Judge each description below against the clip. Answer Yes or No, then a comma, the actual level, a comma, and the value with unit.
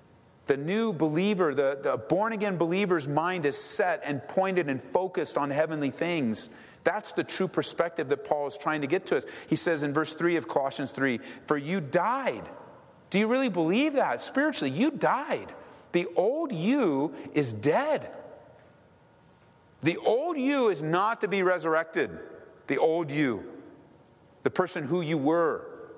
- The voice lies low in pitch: No, medium, 170 Hz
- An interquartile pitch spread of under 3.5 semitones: No, average, 4.6 semitones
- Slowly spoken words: No, average, 160 wpm